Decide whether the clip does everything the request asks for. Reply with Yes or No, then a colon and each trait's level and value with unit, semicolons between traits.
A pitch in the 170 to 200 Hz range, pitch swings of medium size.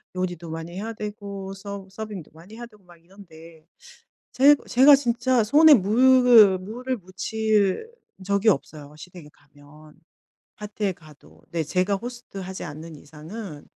Yes: high, 195 Hz; average, 5.0 semitones